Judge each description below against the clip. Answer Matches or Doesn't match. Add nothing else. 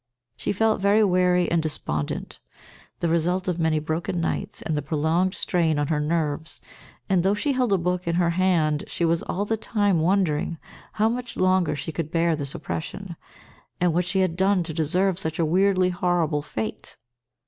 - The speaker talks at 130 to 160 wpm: Doesn't match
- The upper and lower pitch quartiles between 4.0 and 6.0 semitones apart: Doesn't match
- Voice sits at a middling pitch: Matches